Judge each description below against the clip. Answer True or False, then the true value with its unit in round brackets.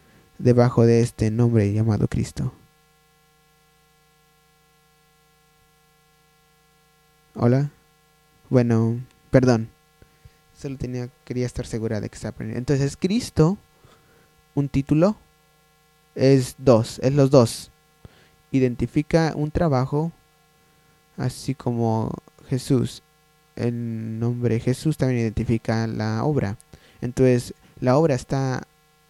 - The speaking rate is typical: False (90 wpm)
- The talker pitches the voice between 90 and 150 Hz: True (140 Hz)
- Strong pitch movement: False (4.1 semitones)